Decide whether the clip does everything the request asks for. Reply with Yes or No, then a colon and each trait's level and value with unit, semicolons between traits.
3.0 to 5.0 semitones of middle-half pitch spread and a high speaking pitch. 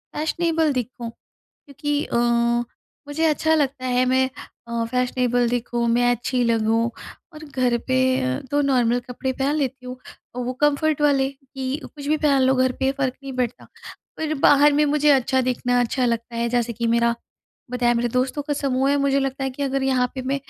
No: narrow, 2.5 semitones; very high, 260 Hz